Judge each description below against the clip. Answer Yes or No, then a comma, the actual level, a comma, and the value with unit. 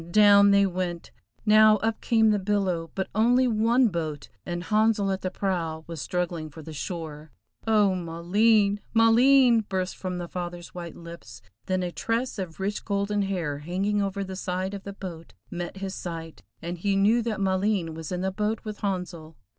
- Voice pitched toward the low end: No, high, 190 Hz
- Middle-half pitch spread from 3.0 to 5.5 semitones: Yes, average, 3.4 semitones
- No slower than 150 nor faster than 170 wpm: No, average, 180 wpm